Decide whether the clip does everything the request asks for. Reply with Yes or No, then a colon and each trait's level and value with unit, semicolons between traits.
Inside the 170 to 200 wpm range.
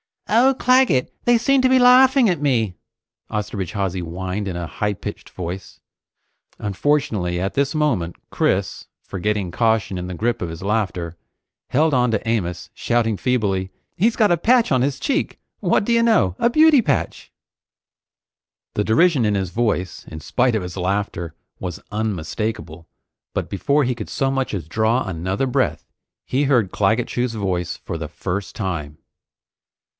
No: average, 160 wpm